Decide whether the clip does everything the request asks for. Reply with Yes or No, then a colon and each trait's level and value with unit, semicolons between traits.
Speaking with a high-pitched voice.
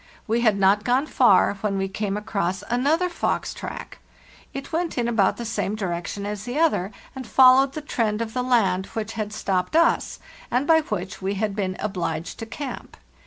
Yes: high, 215 Hz